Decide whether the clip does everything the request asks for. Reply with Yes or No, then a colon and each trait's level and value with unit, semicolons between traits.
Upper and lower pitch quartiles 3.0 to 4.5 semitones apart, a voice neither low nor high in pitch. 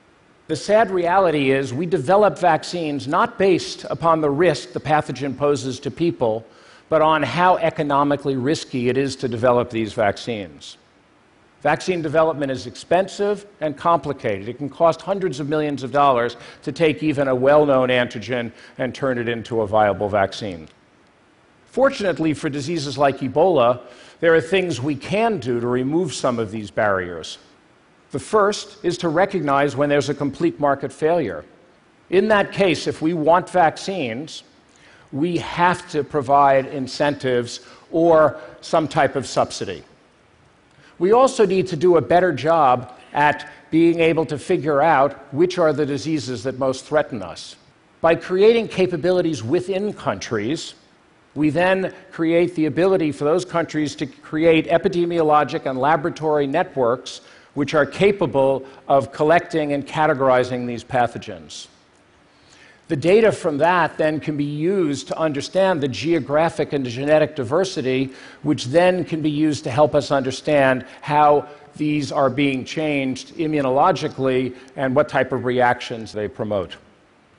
Yes: average, 3.9 semitones; medium, 150 Hz